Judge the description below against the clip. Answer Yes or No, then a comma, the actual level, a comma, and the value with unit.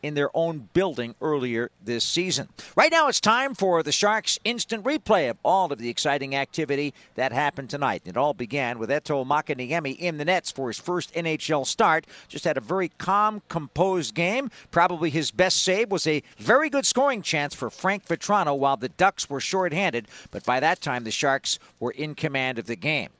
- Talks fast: No, average, 195 wpm